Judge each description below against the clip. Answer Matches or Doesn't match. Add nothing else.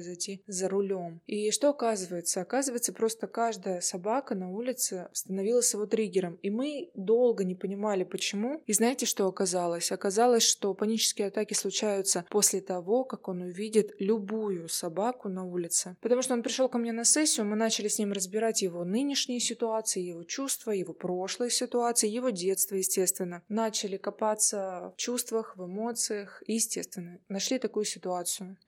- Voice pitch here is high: Matches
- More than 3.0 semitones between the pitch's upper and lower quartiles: Matches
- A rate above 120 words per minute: Matches